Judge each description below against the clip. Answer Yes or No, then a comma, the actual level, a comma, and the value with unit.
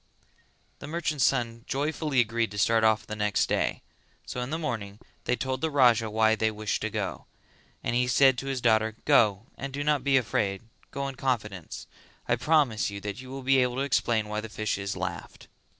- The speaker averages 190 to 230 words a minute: Yes, average, 200 wpm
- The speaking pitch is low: Yes, low, 120 Hz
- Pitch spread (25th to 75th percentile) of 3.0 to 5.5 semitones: Yes, average, 4.0 semitones